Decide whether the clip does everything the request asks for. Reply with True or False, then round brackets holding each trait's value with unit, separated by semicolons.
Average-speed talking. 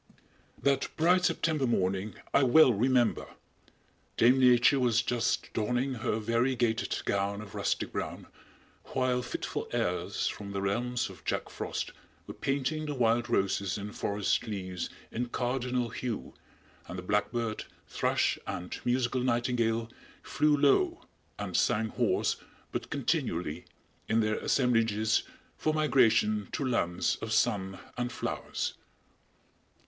False (125 wpm)